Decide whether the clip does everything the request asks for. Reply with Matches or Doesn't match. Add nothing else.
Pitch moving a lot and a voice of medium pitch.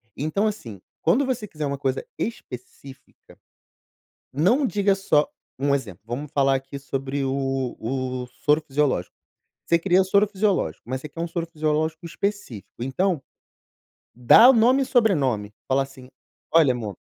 Matches